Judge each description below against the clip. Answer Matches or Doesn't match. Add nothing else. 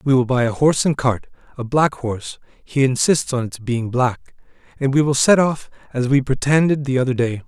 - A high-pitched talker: Doesn't match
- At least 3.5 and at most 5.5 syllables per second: Matches